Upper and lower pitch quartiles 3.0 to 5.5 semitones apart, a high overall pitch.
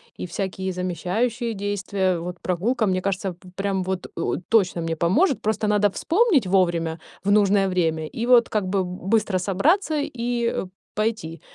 Yes: average, 3.7 semitones; high, 195 Hz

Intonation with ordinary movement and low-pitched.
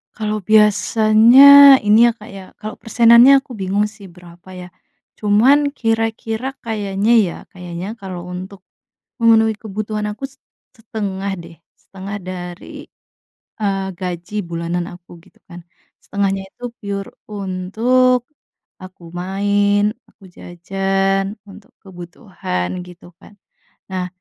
No: average, 3.1 semitones; high, 200 Hz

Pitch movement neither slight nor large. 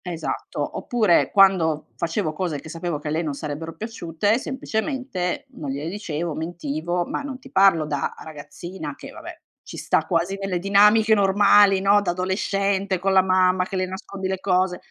Yes: average, 3.3 semitones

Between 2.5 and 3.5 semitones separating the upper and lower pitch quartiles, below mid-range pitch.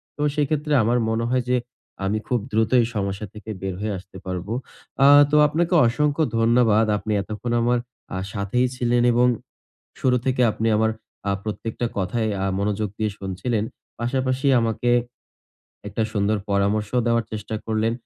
Yes: average, 2.8 semitones; low, 110 Hz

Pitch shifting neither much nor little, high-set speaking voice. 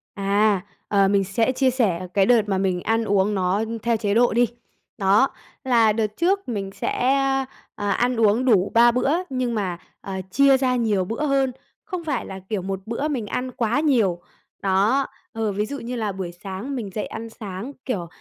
Yes: average, 4.3 semitones; high, 220 Hz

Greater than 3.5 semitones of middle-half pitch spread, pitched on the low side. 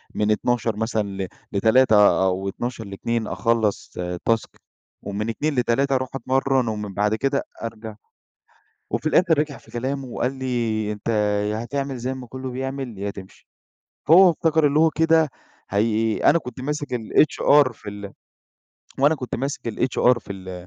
Yes: average, 4.2 semitones; low, 120 Hz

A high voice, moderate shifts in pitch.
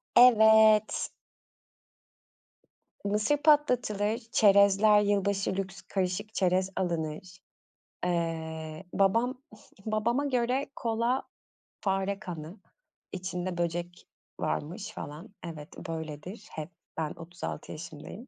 Yes: high, 195 Hz; average, 4.4 semitones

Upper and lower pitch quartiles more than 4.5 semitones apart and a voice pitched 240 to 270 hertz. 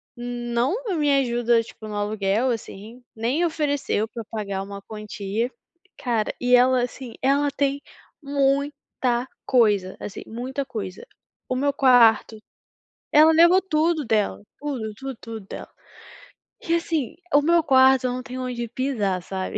No: average, 4.1 semitones; high, 245 Hz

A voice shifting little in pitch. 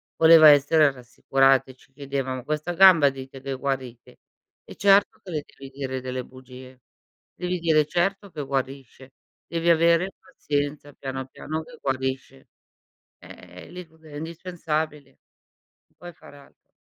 No: average, 3.7 semitones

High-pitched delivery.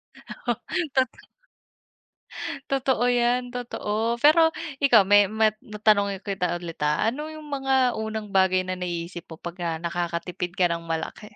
Yes: high, 200 Hz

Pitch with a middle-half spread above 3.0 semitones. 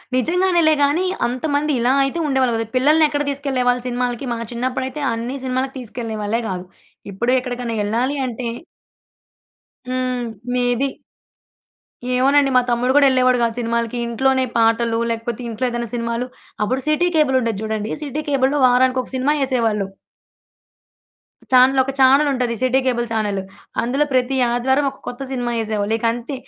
No: narrow, 2.4 semitones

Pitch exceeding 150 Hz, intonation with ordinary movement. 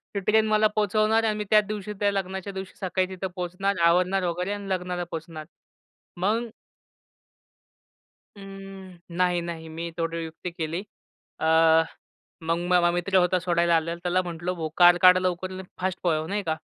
No: medium, 185 Hz; narrow, 2.3 semitones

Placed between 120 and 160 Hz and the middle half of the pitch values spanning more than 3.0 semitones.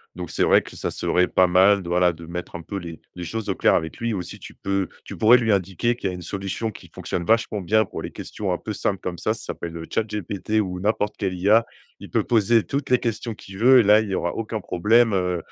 No: low, 100 Hz; average, 3.6 semitones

